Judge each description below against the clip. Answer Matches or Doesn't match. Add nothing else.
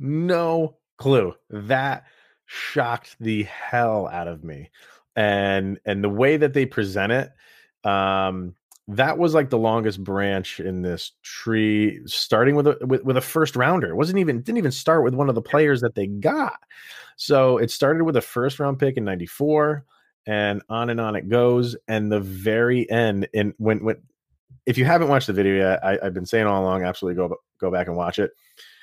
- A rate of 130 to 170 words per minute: Doesn't match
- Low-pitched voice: Matches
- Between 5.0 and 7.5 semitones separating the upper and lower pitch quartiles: Matches